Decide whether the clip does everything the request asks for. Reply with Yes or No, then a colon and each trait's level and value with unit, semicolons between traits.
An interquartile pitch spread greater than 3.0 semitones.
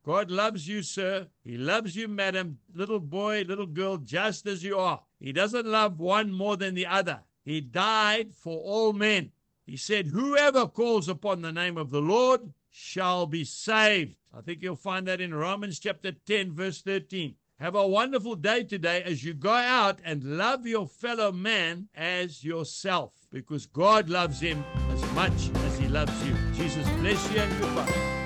Yes: average, 4.2 semitones